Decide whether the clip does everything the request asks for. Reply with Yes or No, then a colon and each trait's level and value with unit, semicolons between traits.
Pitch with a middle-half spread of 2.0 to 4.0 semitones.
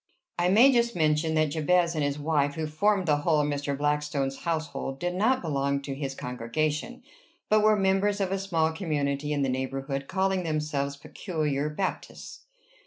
No: average, 4.4 semitones